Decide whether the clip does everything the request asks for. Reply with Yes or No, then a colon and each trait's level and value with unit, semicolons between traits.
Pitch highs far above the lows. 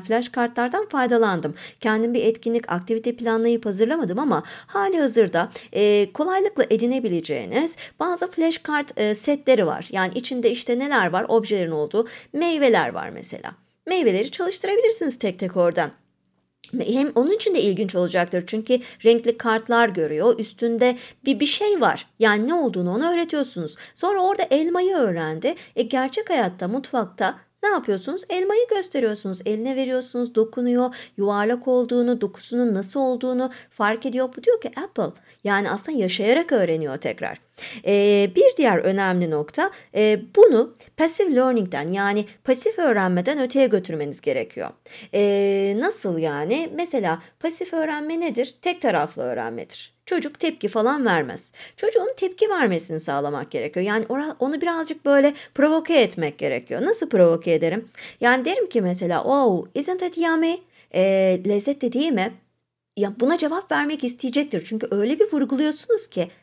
Yes: wide, 7.2 semitones